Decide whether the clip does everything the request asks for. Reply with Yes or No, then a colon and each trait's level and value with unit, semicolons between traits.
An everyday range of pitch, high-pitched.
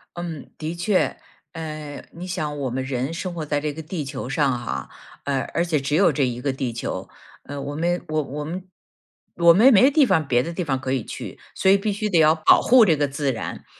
No: average, 4.0 semitones; medium, 155 Hz